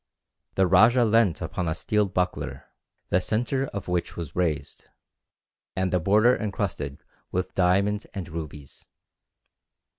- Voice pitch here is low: Yes, very low, 95 Hz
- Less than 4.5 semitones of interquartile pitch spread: Yes, average, 3.5 semitones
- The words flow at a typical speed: No, slow, 125 wpm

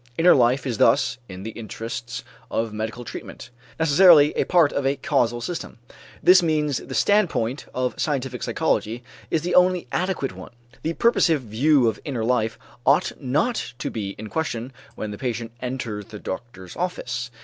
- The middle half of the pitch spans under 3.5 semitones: No, average, 5.3 semitones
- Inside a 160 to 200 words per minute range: Yes, average, 165 wpm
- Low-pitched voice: Yes, low, 125 Hz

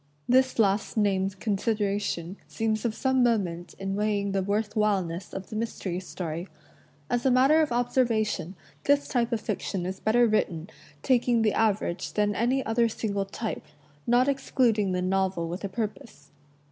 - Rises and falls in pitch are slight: No, average, 3.6 semitones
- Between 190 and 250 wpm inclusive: No, average, 160 wpm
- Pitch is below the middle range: No, high, 210 Hz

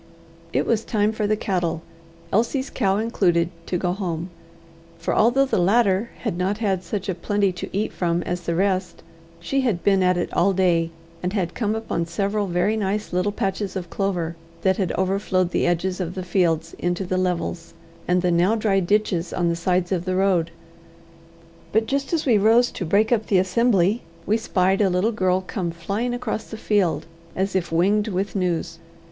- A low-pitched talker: No, high, 190 Hz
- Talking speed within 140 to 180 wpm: No, average, 190 wpm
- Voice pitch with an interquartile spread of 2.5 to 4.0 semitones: Yes, average, 3.0 semitones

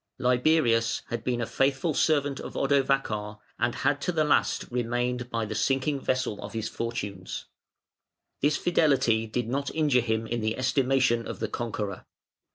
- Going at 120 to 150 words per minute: No, average, 160 wpm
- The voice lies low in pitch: Yes, low, 125 Hz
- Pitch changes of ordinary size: Yes, average, 3.2 semitones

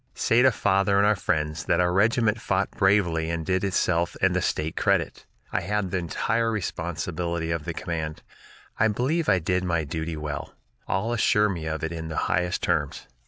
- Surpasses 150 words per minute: Yes, average, 190 wpm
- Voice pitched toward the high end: No, very low, 90 Hz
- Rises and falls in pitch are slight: No, average, 4.1 semitones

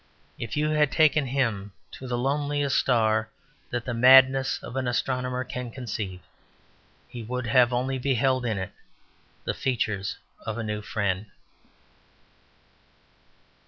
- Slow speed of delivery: Yes, slow, 130 wpm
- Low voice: Yes, low, 125 Hz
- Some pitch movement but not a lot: Yes, average, 3.2 semitones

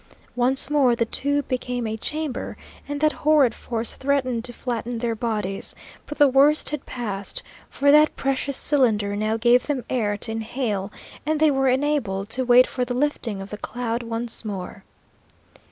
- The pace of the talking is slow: No, average, 170 wpm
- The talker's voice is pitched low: No, high, 245 Hz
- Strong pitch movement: No, average, 3.9 semitones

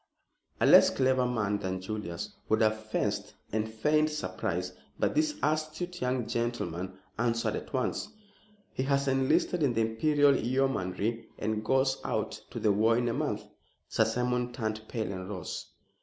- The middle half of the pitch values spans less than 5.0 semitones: Yes, average, 3.7 semitones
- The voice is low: Yes, low, 120 Hz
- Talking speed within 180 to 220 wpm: No, average, 155 wpm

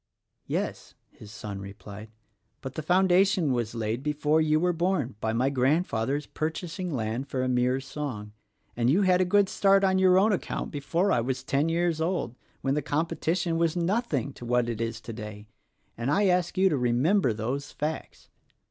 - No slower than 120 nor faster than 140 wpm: No, average, 190 wpm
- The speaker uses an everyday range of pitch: No, wide, 6.7 semitones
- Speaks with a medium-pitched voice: Yes, medium, 145 Hz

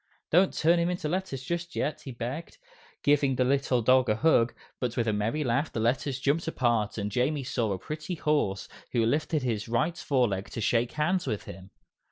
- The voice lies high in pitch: No, low, 130 Hz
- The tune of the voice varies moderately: Yes, average, 4.9 semitones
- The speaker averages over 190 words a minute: Yes, average, 200 wpm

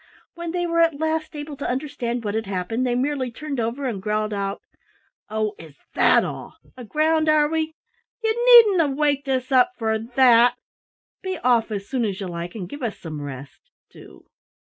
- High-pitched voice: Yes, very high, 255 Hz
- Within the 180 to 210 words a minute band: Yes, average, 190 wpm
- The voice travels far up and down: Yes, wide, 6.1 semitones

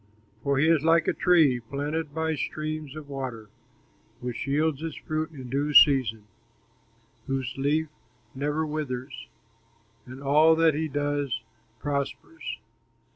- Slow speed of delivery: Yes, slow, 130 wpm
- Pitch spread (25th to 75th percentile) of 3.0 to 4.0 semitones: No, narrow, 2.6 semitones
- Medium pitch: Yes, medium, 145 Hz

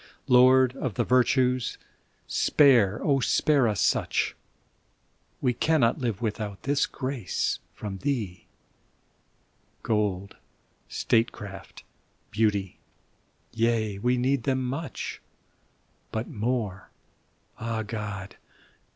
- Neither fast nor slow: No, slow, 95 wpm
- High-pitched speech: No, low, 115 Hz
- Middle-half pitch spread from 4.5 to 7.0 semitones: No, average, 3.7 semitones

